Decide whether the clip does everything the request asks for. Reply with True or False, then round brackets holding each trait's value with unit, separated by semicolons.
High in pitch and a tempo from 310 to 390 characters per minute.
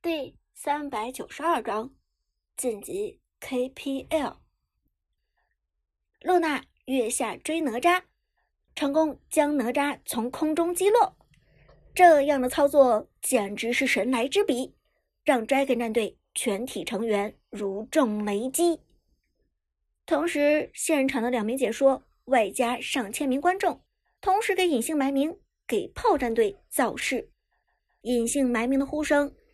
False (275 Hz; 190 characters per minute)